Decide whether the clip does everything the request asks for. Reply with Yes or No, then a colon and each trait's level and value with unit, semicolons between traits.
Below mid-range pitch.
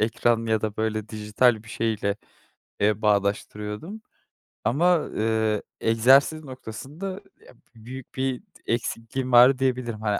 Yes: low, 115 Hz